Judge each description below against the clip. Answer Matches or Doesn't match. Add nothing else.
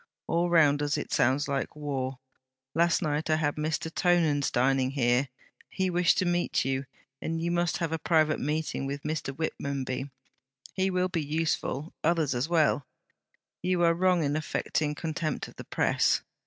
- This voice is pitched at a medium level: Matches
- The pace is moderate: Matches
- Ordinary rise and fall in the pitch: Matches